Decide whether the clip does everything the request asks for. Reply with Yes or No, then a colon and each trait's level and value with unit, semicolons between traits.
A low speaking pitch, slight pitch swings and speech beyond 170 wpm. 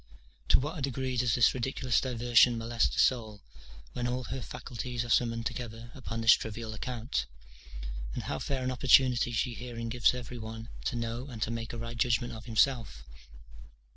Yes: low, 120 Hz; narrow, 1.7 semitones; average, 180 wpm